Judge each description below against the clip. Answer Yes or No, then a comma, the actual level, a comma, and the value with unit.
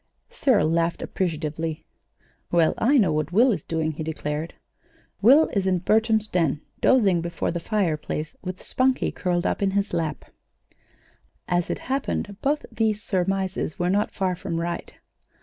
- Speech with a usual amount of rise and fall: Yes, average, 4.2 semitones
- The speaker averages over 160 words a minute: No, average, 150 wpm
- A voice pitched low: No, medium, 180 Hz